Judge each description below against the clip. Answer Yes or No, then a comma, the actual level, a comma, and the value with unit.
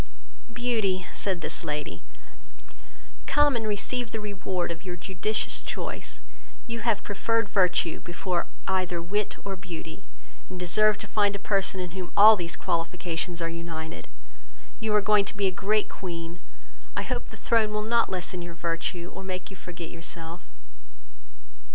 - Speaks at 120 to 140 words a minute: No, average, 155 wpm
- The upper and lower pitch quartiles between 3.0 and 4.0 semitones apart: Yes, average, 3.5 semitones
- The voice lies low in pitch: No, medium, 185 Hz